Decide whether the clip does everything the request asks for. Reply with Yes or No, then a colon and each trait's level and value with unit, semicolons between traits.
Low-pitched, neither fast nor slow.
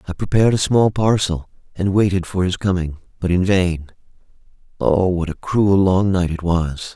Yes: very low, 90 Hz; average, 180 wpm